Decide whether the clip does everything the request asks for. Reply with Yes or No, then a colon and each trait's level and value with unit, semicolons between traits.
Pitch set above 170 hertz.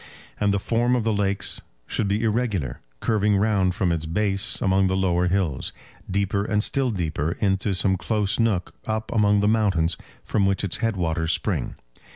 No: low, 100 Hz